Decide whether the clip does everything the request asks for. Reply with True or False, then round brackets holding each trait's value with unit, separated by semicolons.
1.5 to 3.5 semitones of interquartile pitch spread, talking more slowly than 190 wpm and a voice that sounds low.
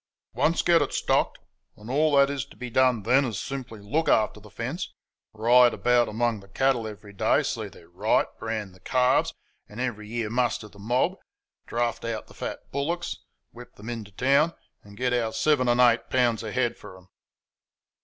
False (3.2 semitones; 195 wpm; 120 Hz)